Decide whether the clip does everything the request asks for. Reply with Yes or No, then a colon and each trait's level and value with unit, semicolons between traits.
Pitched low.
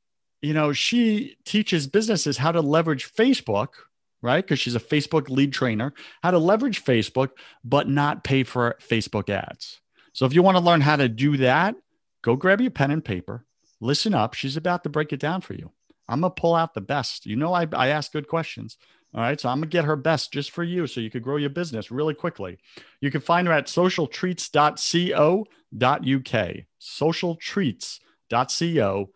No: medium, 150 Hz